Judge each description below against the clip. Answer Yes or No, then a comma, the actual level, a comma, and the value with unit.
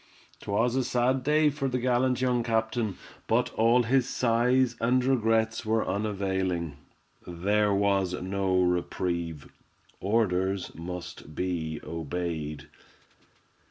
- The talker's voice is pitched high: No, low, 105 Hz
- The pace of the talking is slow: Yes, slow, 105 wpm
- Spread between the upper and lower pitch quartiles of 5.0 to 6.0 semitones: Yes, average, 5.3 semitones